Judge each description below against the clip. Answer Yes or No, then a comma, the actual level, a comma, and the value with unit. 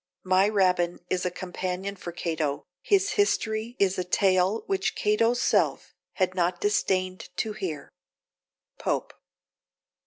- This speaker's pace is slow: Yes, slow, 125 wpm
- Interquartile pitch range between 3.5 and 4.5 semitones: No, average, 2.7 semitones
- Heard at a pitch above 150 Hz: Yes, medium, 185 Hz